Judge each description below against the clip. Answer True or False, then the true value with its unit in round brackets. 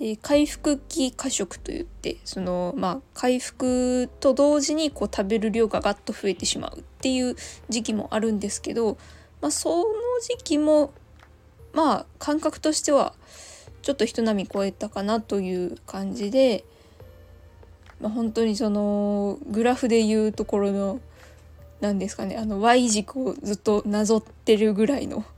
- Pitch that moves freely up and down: False (4.9 semitones)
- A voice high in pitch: True (220 Hz)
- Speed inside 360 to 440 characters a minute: False (285 characters per minute)